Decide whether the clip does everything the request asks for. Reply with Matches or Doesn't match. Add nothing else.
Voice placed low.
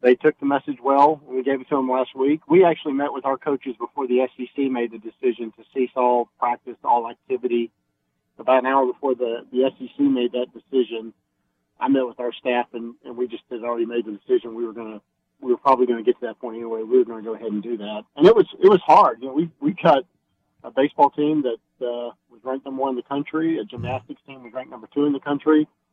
Matches